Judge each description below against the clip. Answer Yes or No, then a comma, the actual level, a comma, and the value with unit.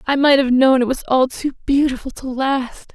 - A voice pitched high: Yes, very high, 265 Hz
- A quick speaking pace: Yes, fast, 225 wpm